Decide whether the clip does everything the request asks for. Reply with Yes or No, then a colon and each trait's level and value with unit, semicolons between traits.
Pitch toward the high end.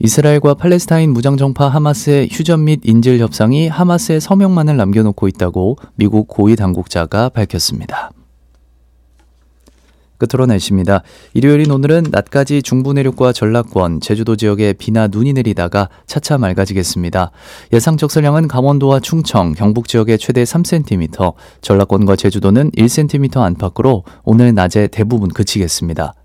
No: low, 115 Hz